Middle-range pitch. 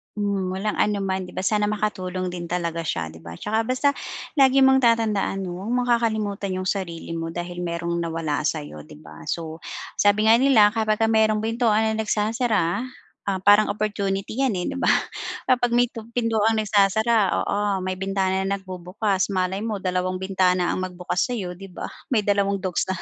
No: high, 200 Hz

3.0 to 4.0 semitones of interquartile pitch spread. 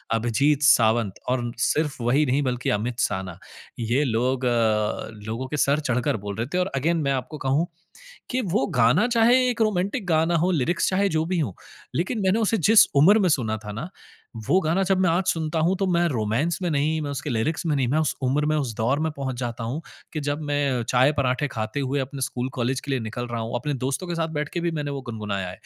No: average, 5.3 semitones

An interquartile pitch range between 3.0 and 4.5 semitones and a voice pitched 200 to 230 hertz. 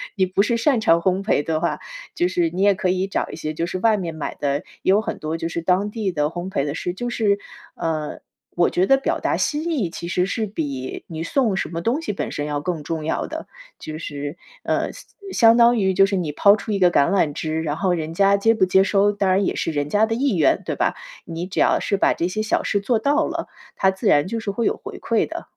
No: average, 4.2 semitones; medium, 185 Hz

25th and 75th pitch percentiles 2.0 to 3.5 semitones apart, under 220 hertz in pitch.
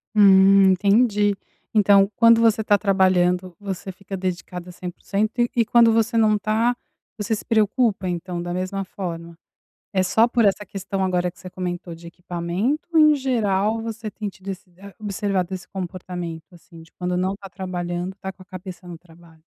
Yes: average, 2.9 semitones; high, 190 Hz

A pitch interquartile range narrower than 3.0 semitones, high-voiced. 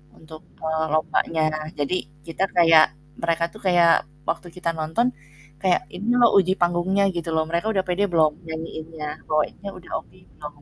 No: narrow, 2.6 semitones; medium, 165 Hz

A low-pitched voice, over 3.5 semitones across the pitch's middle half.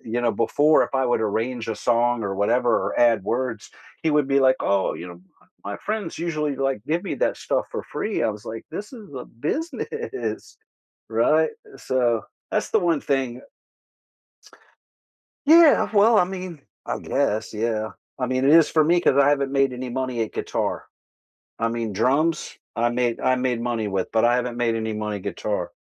Yes: low, 125 Hz; average, 5.1 semitones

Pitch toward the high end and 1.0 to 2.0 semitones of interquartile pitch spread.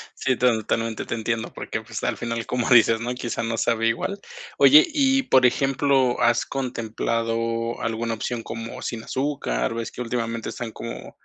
No: low, 115 Hz; narrow, 1.7 semitones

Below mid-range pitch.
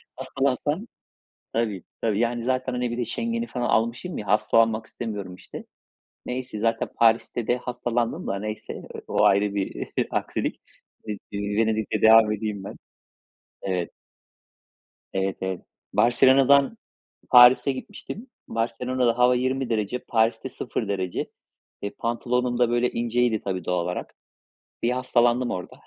Yes: low, 115 Hz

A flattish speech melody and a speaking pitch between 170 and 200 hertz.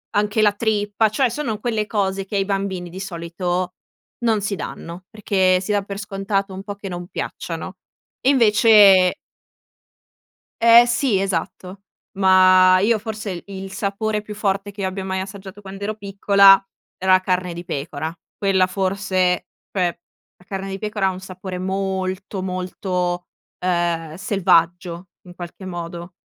Yes: narrow, 1.9 semitones; high, 190 Hz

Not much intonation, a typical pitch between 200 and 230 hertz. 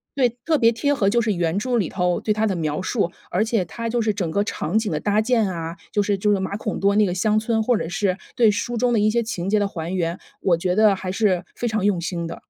No: average, 3.5 semitones; high, 205 Hz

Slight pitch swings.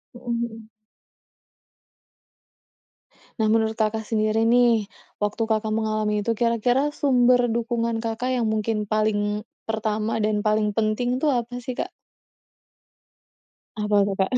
Yes: narrow, 1.7 semitones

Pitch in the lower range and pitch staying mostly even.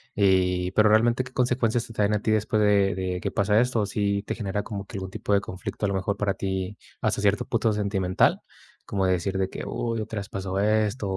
Yes: low, 100 Hz; narrow, 2.0 semitones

